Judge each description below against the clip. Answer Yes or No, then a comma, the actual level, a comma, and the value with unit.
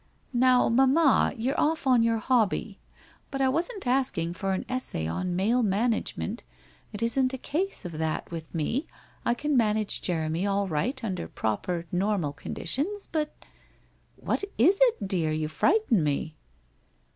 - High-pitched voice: Yes, high, 225 Hz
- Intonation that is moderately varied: No, wide, 7.0 semitones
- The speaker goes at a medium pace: Yes, average, 160 wpm